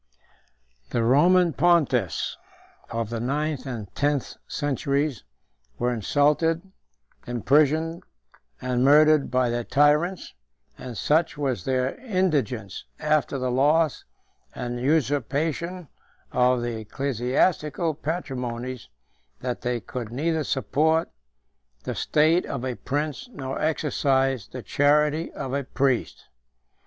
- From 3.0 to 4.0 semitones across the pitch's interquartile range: Yes, average, 3.7 semitones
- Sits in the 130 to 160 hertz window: Yes, medium, 140 Hz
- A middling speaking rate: No, slow, 105 wpm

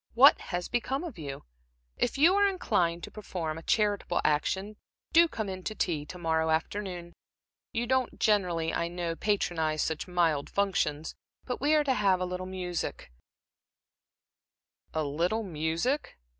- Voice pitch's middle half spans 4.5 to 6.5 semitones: Yes, average, 5.1 semitones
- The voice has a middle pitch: Yes, medium, 180 Hz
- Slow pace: No, average, 155 wpm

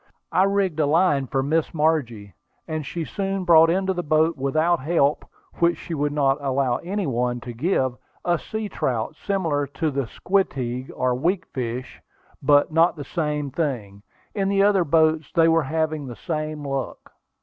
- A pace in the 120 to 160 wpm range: No, average, 170 wpm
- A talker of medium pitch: Yes, medium, 155 Hz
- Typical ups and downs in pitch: Yes, average, 4.2 semitones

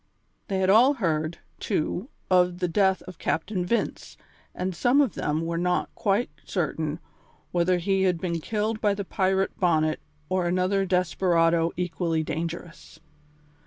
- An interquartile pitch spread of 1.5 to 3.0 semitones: Yes, narrow, 2.5 semitones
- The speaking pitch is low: No, medium, 180 Hz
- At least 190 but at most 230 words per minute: No, average, 145 wpm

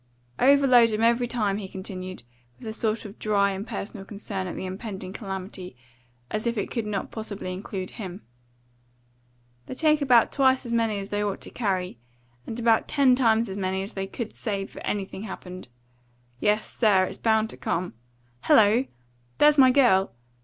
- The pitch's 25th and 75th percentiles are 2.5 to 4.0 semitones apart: Yes, average, 3.4 semitones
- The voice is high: Yes, high, 210 Hz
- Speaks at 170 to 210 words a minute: Yes, average, 175 wpm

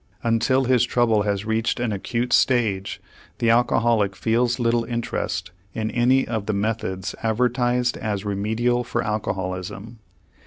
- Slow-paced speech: Yes, slow, 130 wpm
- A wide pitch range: No, average, 2.8 semitones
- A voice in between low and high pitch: No, low, 115 Hz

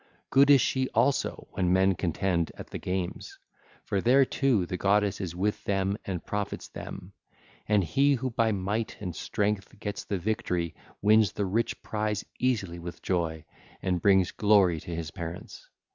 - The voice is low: Yes, low, 100 Hz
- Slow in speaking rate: No, average, 165 wpm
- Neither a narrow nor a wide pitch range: Yes, average, 3.3 semitones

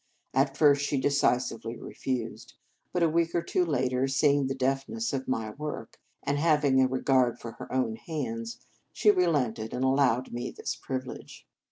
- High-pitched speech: No, low, 135 Hz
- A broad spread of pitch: No, average, 2.7 semitones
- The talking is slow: No, average, 165 wpm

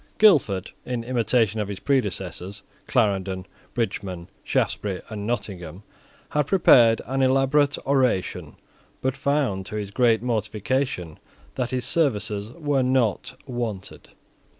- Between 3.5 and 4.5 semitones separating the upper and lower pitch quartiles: No, average, 4.9 semitones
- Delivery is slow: Yes, slow, 115 wpm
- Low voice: Yes, low, 115 Hz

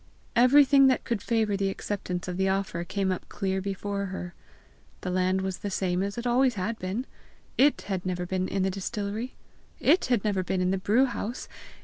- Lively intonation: No, average, 3.6 semitones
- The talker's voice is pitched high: Yes, high, 195 Hz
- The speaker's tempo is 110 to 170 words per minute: No, average, 200 wpm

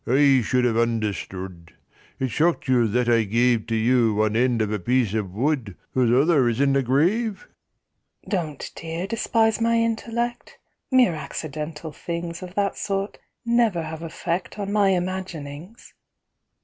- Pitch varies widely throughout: Yes, wide, 8.0 semitones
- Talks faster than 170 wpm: No, average, 150 wpm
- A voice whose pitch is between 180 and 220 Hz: No, medium, 150 Hz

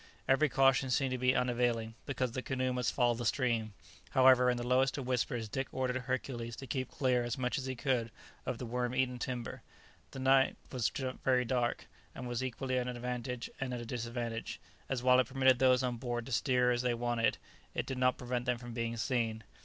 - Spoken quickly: Yes, fast, 210 wpm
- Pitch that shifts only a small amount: Yes, narrow, 1.4 semitones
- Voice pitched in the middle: No, low, 125 Hz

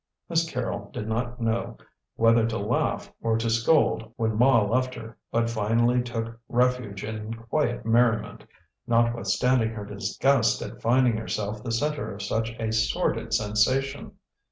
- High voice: No, low, 115 Hz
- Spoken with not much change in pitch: Yes, narrow, 1.8 semitones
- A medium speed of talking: Yes, average, 145 wpm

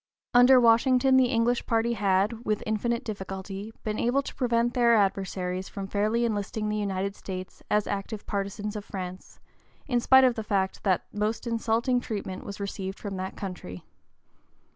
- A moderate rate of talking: Yes, average, 165 wpm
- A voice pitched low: No, high, 210 Hz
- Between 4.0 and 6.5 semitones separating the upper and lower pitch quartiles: No, average, 3.2 semitones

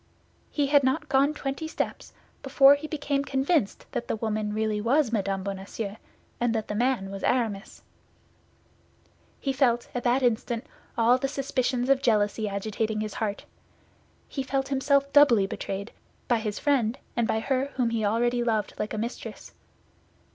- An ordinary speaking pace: Yes, average, 160 wpm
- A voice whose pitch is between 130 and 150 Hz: No, high, 240 Hz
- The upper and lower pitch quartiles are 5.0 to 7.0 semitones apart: No, average, 4.0 semitones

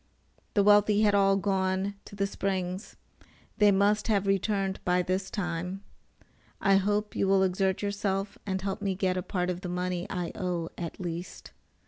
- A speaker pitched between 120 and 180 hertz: No, high, 195 Hz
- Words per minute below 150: No, average, 170 wpm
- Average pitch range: No, narrow, 1.8 semitones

